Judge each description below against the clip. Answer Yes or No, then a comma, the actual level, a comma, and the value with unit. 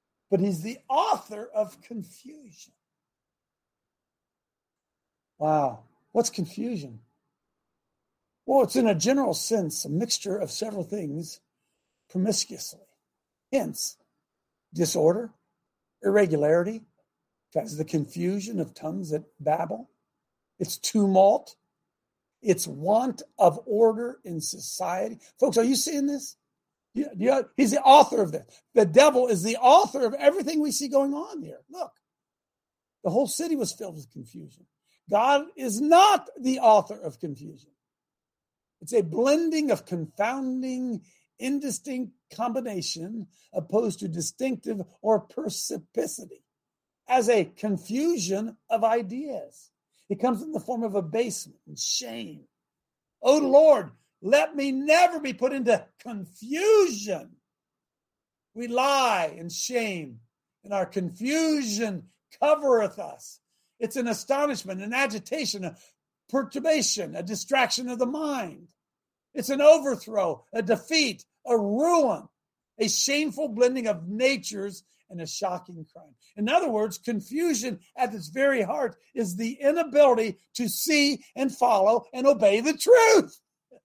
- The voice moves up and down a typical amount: No, wide, 6.2 semitones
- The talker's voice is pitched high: Yes, high, 230 Hz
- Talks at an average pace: No, slow, 120 wpm